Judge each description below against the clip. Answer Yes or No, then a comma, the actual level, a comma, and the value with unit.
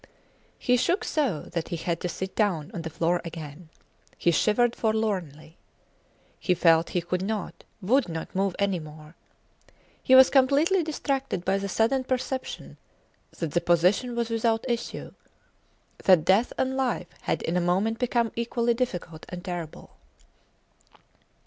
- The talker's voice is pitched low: No, high, 195 Hz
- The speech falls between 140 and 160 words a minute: Yes, average, 150 wpm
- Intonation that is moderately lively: No, wide, 5.9 semitones